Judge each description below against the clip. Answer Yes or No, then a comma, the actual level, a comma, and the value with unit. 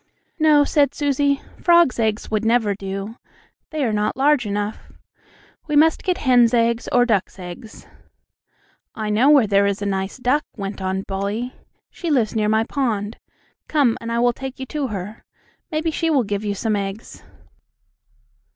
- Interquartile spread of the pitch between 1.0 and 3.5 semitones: No, average, 5.3 semitones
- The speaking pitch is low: No, high, 230 Hz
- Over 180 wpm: No, average, 170 wpm